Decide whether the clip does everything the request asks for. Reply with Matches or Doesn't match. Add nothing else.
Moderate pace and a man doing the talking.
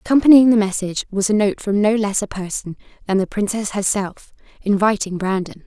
Doesn't match